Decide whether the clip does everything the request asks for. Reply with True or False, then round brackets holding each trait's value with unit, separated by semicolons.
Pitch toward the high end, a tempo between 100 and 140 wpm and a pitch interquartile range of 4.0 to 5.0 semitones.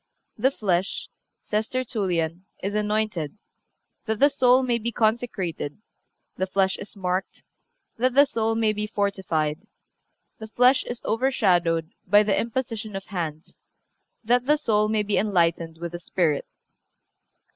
True (210 Hz; 135 wpm; 4.3 semitones)